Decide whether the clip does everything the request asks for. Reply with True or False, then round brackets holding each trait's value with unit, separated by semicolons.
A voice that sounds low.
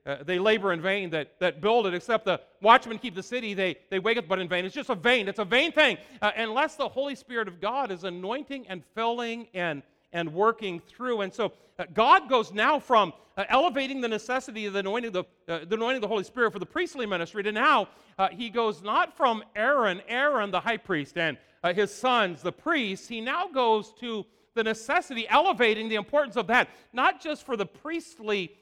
False (220 Hz)